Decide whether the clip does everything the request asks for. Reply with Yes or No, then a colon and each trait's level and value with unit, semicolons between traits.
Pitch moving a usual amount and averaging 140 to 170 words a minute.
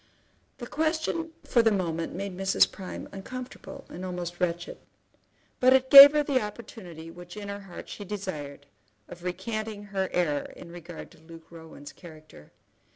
Yes: average, 4.7 semitones; average, 160 wpm